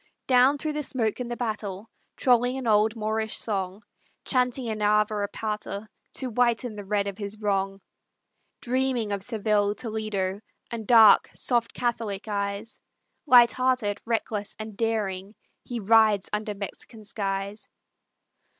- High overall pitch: Yes, high, 215 Hz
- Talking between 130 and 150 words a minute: Yes, average, 140 wpm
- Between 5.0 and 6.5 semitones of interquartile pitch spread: No, average, 2.7 semitones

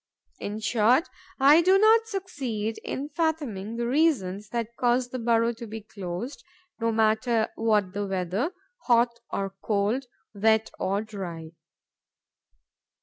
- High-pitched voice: Yes, high, 225 Hz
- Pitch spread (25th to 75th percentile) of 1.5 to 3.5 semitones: No, average, 4.0 semitones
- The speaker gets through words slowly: Yes, slow, 130 wpm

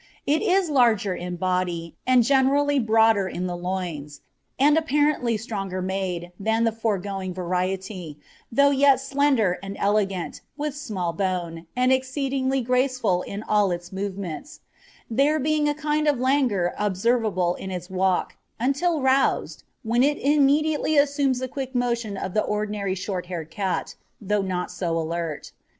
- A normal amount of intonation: No, wide, 6.7 semitones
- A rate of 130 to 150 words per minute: Yes, average, 145 wpm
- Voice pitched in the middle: No, high, 215 Hz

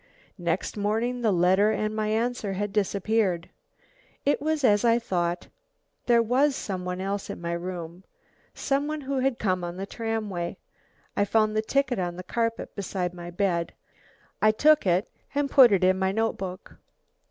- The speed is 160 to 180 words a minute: Yes, average, 170 wpm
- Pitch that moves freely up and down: No, average, 4.2 semitones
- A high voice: Yes, high, 205 Hz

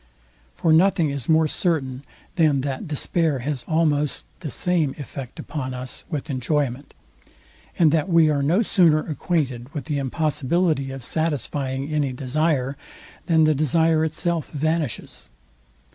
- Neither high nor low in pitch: Yes, medium, 150 Hz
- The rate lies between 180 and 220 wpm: No, slow, 135 wpm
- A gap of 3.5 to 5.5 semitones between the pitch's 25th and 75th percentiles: No, average, 3.1 semitones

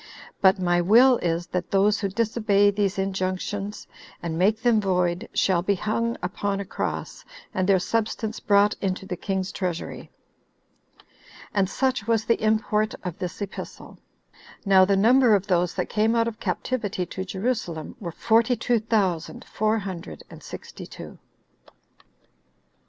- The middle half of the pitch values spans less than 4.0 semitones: Yes, average, 2.9 semitones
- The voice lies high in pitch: Yes, high, 200 Hz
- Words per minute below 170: Yes, average, 150 wpm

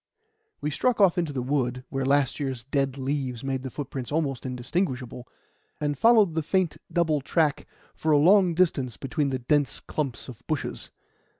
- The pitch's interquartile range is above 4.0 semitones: No, average, 3.6 semitones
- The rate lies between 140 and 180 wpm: Yes, average, 170 wpm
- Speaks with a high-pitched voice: No, medium, 145 Hz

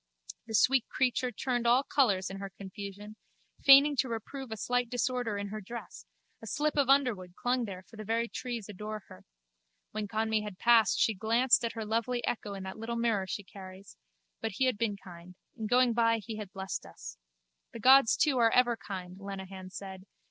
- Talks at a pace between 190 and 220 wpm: Yes, average, 195 wpm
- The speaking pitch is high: Yes, high, 220 Hz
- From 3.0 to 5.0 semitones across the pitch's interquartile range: Yes, average, 3.7 semitones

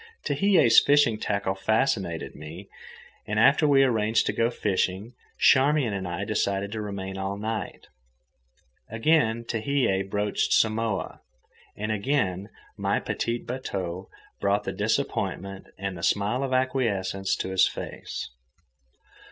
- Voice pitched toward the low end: Yes, low, 105 Hz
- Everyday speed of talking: No, slow, 125 wpm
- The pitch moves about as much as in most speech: Yes, average, 3.7 semitones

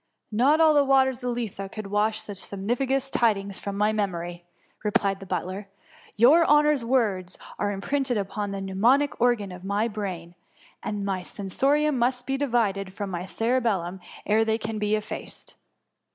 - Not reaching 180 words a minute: Yes, average, 165 wpm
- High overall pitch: Yes, high, 215 Hz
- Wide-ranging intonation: No, average, 4.2 semitones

